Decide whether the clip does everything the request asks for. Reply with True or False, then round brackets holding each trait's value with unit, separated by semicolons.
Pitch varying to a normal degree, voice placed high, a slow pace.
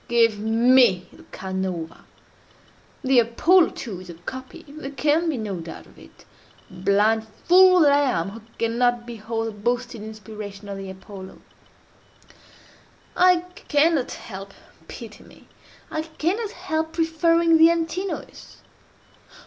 False (7.7 semitones; 240 Hz; 115 wpm)